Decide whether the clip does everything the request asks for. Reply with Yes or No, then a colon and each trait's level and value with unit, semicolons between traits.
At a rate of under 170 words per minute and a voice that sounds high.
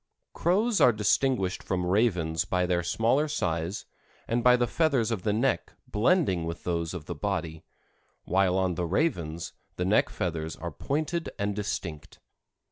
No: average, 155 wpm; very low, 95 Hz